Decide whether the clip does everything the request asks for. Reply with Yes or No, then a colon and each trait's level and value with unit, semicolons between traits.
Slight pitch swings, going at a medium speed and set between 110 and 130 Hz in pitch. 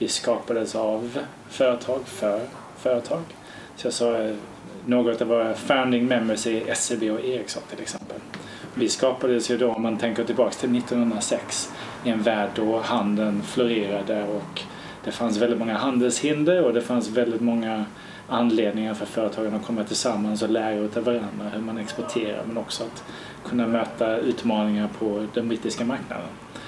Yes: narrow, 2.0 semitones; average, 150 wpm; low, 115 Hz